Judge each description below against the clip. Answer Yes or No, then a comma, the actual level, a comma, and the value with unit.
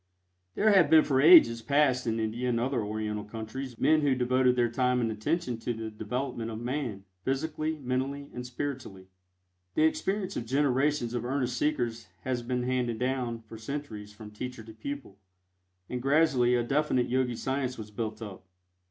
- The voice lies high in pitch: No, low, 125 Hz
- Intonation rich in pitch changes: No, average, 3.5 semitones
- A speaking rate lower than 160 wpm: No, average, 170 wpm